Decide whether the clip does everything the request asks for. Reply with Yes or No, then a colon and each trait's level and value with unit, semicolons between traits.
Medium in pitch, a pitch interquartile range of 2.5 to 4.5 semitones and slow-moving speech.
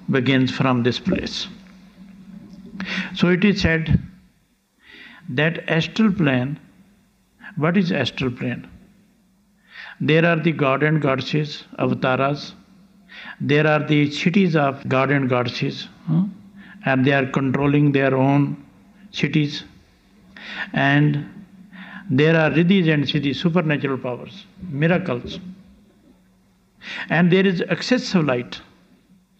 No: medium, 170 Hz; wide, 5.5 semitones; slow, 100 wpm